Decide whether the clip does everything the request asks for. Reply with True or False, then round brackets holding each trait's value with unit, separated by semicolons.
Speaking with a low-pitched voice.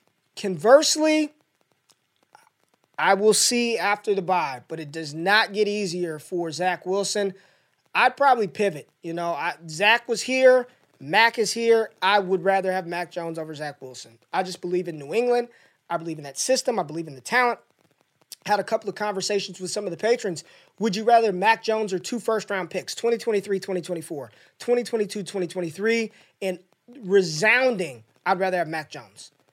False (195 Hz)